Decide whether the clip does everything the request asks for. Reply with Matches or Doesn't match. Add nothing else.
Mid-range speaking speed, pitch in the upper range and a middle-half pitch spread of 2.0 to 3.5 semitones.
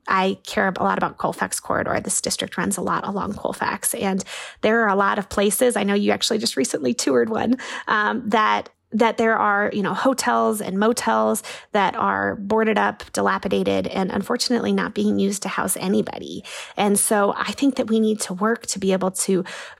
Matches